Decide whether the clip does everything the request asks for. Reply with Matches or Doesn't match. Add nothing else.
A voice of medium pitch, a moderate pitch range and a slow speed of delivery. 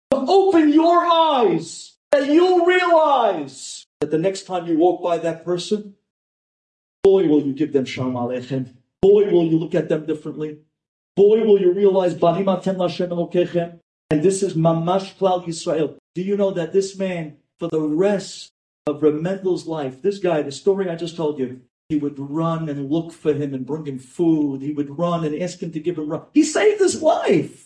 Doesn't match